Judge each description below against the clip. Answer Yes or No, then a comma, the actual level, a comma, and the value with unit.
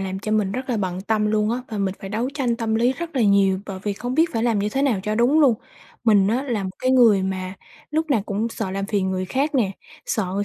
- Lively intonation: No, average, 4.0 semitones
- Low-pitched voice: No, high, 215 Hz